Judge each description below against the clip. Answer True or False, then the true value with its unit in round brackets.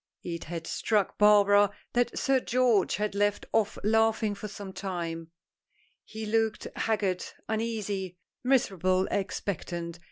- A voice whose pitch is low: False (205 Hz)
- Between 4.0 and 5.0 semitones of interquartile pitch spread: False (3.0 semitones)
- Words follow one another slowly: True (120 wpm)